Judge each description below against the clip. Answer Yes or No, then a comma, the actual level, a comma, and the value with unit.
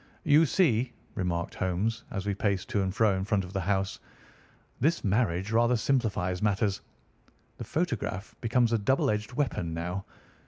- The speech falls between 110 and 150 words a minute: No, average, 160 wpm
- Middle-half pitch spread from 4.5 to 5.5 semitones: No, average, 3.8 semitones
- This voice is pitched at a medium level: No, low, 105 Hz